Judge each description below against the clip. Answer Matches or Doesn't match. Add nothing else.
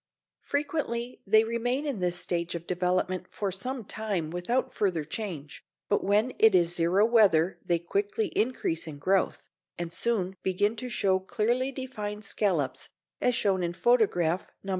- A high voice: Matches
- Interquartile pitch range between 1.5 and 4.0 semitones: Doesn't match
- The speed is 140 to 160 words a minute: Matches